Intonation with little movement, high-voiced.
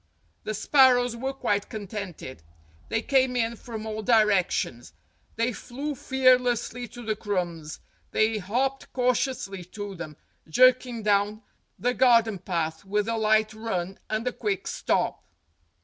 No: average, 3.7 semitones; high, 220 Hz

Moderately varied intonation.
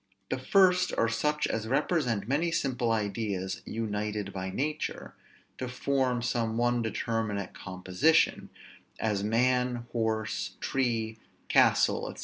Yes: average, 3.3 semitones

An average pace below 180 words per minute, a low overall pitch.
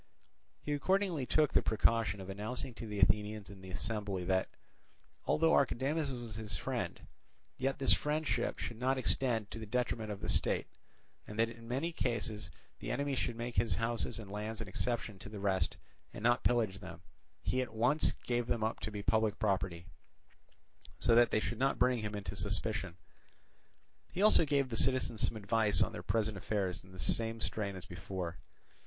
No: average, 185 wpm; low, 110 Hz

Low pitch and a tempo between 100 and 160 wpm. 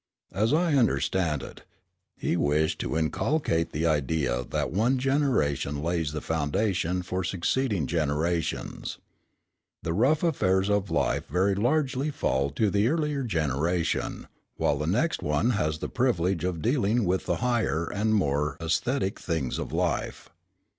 Yes: very low, 90 Hz; average, 140 wpm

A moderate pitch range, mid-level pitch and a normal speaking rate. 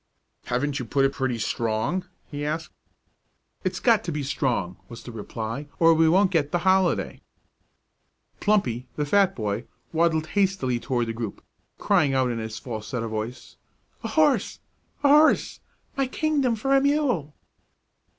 No: wide, 8.1 semitones; medium, 145 Hz; average, 150 wpm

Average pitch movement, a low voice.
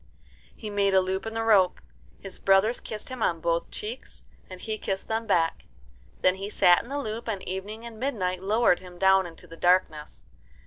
No: average, 3.3 semitones; high, 195 Hz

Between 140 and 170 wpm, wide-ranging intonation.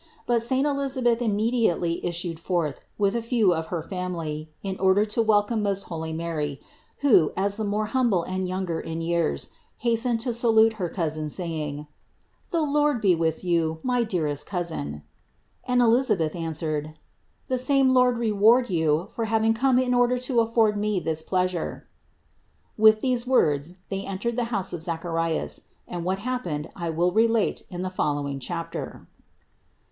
Yes: average, 165 wpm; wide, 6.0 semitones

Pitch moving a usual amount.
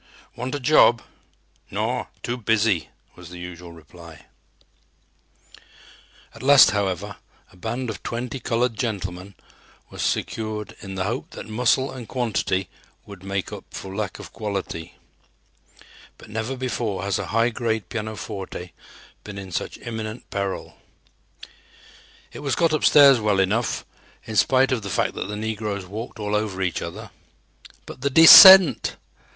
Yes: average, 3.8 semitones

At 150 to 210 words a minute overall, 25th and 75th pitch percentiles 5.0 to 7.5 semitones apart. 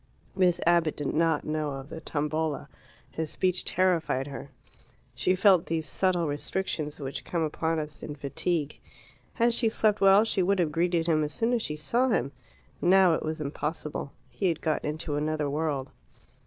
No: average, 175 wpm; average, 3.5 semitones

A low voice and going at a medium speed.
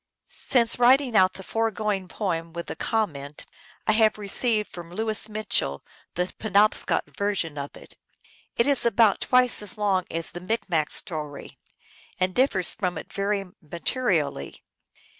No: high, 200 Hz; average, 150 wpm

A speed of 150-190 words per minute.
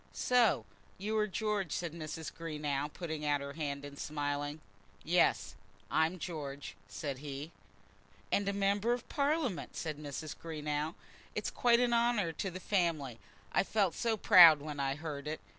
Yes: average, 160 wpm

